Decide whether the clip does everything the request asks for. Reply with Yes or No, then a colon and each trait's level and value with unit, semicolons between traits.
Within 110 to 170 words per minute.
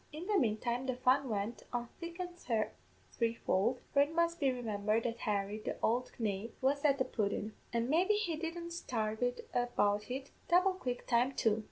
No: average, 185 wpm